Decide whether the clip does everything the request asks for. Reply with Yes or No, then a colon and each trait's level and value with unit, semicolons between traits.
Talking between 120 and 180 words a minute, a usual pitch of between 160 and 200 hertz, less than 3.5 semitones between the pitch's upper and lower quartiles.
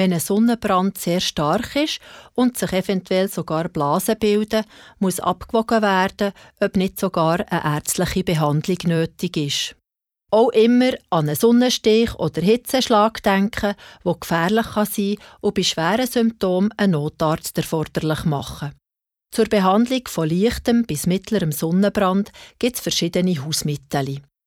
No: average, 135 wpm; high, 190 Hz; average, 4.7 semitones